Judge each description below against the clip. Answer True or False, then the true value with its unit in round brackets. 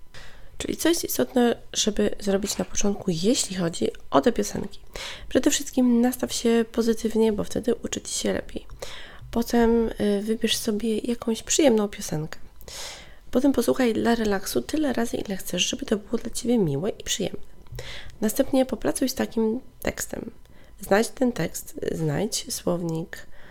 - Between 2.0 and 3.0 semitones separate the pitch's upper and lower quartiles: False (3.8 semitones)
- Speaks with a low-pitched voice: False (230 Hz)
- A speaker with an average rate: True (145 wpm)